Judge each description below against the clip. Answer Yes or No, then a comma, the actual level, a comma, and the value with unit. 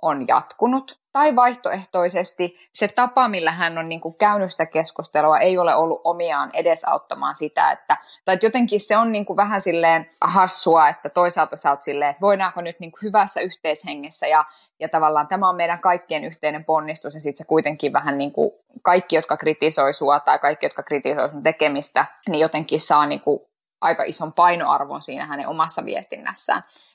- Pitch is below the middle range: No, medium, 165 Hz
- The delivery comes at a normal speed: No, fast, 170 wpm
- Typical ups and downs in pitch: Yes, average, 3.4 semitones